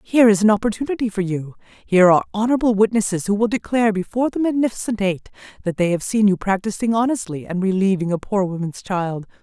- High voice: Yes, high, 205 Hz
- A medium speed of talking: Yes, average, 190 wpm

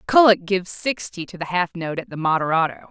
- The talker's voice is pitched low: No, medium, 180 Hz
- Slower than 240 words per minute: Yes, fast, 205 wpm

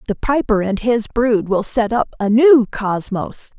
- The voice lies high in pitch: Yes, high, 225 Hz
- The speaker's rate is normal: Yes, average, 185 wpm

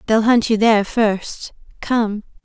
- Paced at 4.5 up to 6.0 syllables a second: No, 3.8 syllables/s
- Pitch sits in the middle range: No, high, 220 Hz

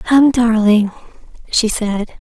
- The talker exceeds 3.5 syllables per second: No, 3.2 syllables/s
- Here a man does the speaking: No, female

